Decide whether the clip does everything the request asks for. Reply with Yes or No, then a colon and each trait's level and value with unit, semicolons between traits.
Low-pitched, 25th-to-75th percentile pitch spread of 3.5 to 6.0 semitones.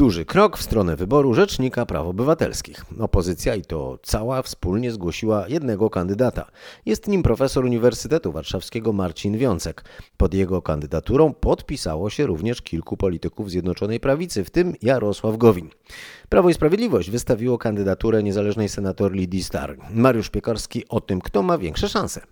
Yes: low, 110 Hz; average, 5.1 semitones